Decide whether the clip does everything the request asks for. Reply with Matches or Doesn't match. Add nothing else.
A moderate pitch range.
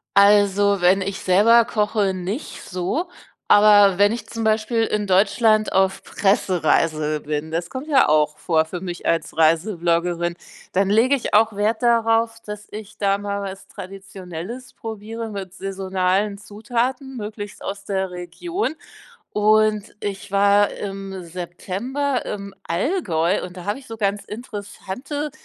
Matches